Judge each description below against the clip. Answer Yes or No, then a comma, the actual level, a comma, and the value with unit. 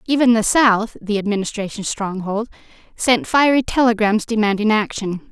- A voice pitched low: No, high, 220 Hz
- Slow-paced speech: Yes, slow, 125 wpm